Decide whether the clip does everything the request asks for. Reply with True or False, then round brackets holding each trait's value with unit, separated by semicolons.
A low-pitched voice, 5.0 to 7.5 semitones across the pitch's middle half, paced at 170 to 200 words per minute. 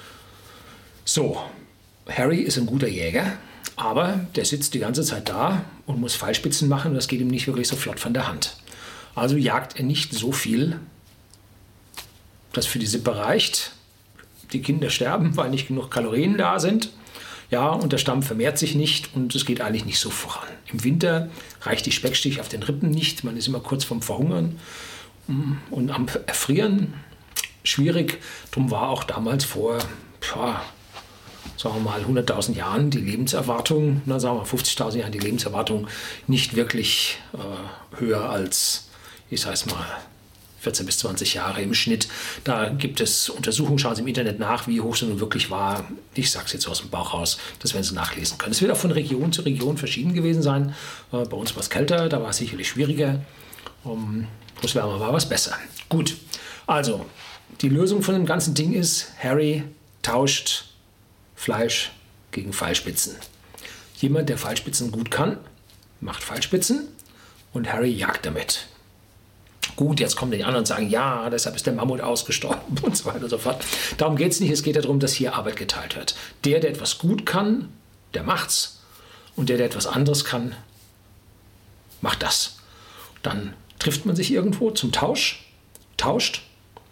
True (125 Hz; 5.4 semitones; 175 wpm)